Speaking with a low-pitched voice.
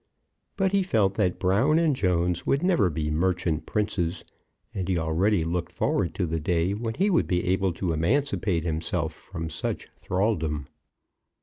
Yes: very low, 90 Hz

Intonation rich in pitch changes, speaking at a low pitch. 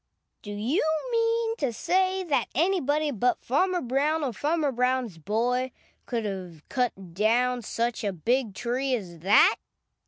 No: wide, 5.9 semitones; very high, 250 Hz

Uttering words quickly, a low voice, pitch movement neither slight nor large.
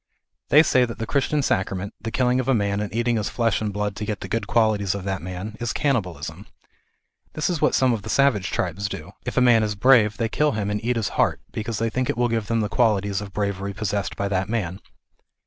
Yes: fast, 245 wpm; low, 110 Hz; average, 3.1 semitones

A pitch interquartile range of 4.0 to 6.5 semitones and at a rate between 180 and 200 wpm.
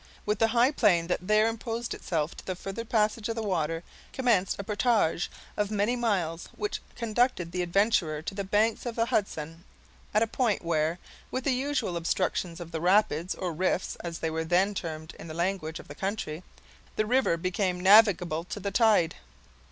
Yes: average, 4.7 semitones; average, 190 wpm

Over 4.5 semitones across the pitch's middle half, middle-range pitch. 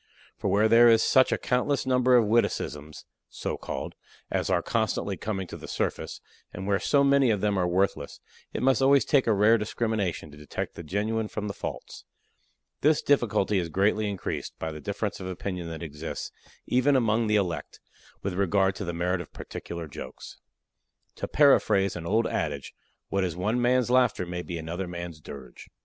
No: average, 5.1 semitones; low, 100 Hz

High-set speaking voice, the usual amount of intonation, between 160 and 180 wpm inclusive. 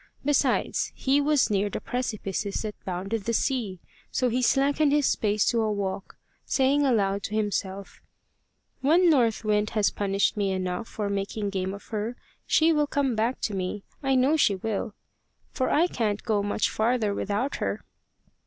Yes: high, 215 Hz; average, 4.6 semitones; average, 170 wpm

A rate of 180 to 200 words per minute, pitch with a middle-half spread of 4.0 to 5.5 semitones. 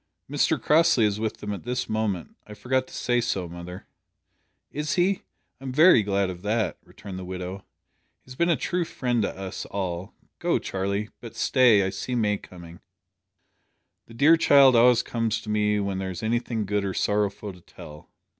Yes: average, 185 wpm; average, 4.3 semitones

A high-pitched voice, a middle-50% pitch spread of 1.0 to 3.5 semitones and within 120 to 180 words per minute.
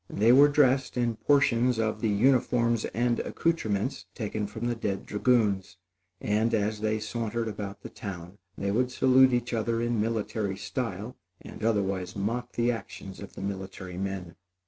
No: low, 110 Hz; average, 3.2 semitones; average, 160 wpm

